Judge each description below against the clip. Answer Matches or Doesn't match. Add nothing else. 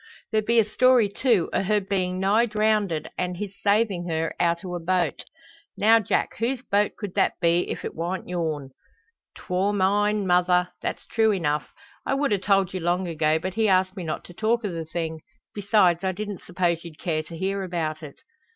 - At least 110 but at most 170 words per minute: Doesn't match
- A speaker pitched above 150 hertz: Matches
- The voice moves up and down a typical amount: Matches